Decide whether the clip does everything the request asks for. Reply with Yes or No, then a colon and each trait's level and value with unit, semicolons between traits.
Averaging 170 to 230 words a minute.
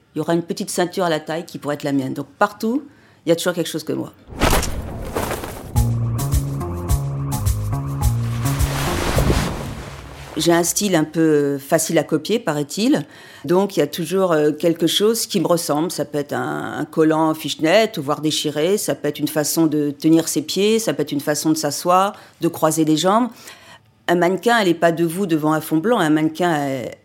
Yes: average, 190 wpm